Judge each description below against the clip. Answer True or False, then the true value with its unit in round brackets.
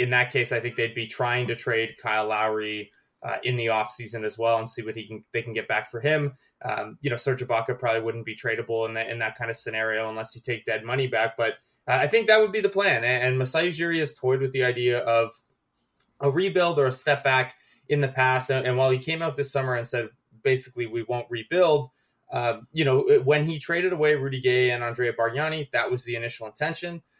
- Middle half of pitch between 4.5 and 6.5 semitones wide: False (3.6 semitones)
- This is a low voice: True (125 Hz)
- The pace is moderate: False (245 wpm)